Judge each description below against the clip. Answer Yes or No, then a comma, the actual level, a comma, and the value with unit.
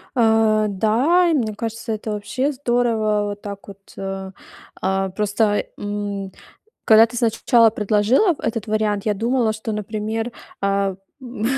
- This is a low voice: No, high, 215 Hz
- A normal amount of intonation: No, narrow, 2.0 semitones